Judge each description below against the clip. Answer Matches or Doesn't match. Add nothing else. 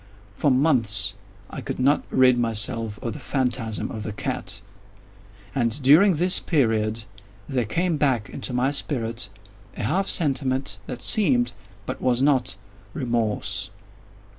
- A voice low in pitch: Matches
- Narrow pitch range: Doesn't match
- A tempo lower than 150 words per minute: Matches